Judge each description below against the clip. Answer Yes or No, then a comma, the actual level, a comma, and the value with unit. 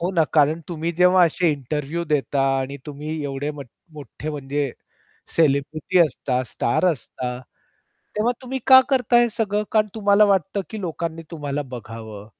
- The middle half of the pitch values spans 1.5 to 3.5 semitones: No, average, 4.9 semitones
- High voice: No, medium, 155 Hz